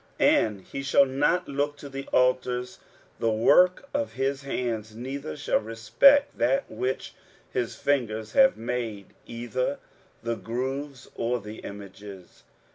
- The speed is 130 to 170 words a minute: Yes, slow, 135 wpm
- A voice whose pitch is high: No, low, 125 Hz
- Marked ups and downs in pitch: No, average, 3.8 semitones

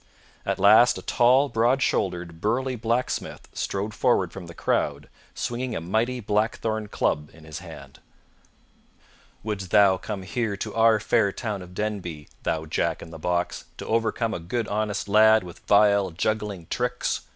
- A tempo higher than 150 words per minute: Yes, average, 160 wpm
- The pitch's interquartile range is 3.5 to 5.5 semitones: Yes, average, 3.9 semitones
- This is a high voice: No, low, 105 Hz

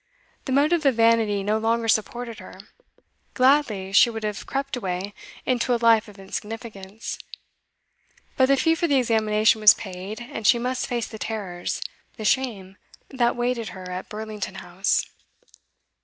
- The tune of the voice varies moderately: Yes, average, 3.3 semitones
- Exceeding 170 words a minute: No, average, 155 wpm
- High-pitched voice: Yes, high, 225 Hz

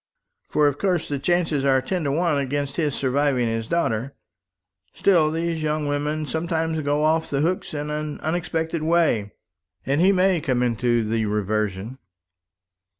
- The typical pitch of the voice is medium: Yes, medium, 150 Hz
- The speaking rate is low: No, average, 155 wpm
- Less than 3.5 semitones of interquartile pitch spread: No, average, 3.8 semitones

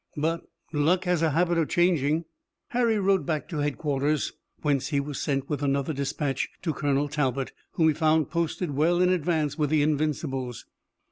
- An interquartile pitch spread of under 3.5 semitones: Yes, average, 2.9 semitones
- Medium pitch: Yes, medium, 150 Hz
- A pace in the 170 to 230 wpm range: Yes, average, 175 wpm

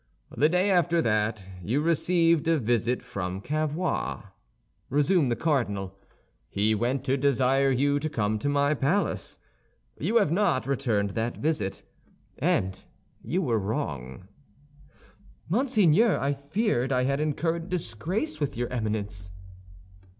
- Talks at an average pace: No, slow, 130 wpm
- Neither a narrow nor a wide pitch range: No, wide, 6.7 semitones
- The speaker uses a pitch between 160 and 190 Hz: No, medium, 140 Hz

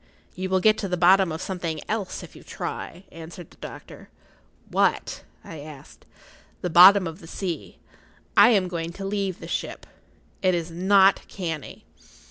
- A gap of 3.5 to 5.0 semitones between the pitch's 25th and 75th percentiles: No, average, 2.8 semitones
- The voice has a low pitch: No, medium, 180 Hz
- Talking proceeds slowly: No, average, 165 wpm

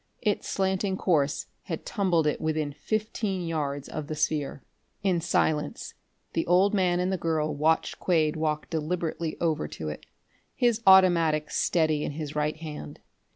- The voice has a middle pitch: Yes, medium, 160 Hz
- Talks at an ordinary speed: Yes, average, 155 wpm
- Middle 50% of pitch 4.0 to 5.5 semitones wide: No, average, 3.1 semitones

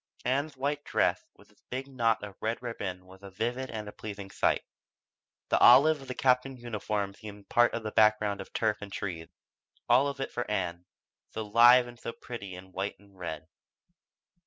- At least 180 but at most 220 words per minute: Yes, average, 190 wpm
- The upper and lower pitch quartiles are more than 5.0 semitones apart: No, average, 4.0 semitones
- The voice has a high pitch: No, low, 110 Hz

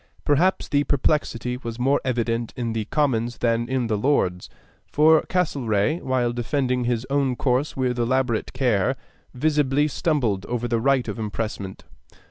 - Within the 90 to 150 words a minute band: Yes, average, 145 wpm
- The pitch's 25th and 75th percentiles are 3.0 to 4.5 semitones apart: Yes, average, 3.3 semitones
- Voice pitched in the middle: No, low, 125 Hz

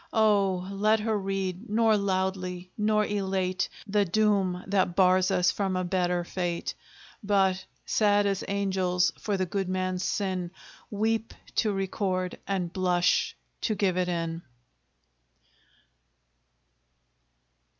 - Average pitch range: No, narrow, 1.9 semitones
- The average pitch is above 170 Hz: Yes, high, 190 Hz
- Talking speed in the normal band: No, slow, 120 wpm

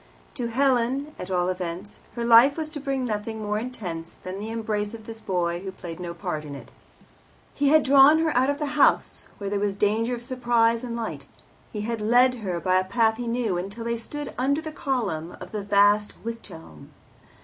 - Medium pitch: No, high, 225 Hz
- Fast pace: Yes, fast, 210 wpm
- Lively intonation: No, average, 4.4 semitones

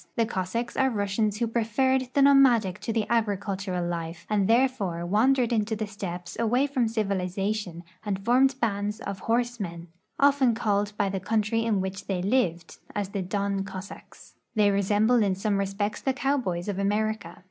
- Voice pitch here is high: Yes, high, 210 Hz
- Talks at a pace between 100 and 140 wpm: No, average, 170 wpm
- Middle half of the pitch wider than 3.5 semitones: No, average, 3.2 semitones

